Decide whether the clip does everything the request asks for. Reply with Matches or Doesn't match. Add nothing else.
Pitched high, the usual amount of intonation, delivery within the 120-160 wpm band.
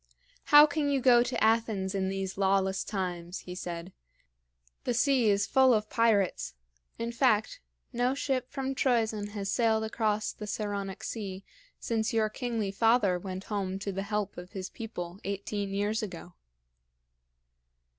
Matches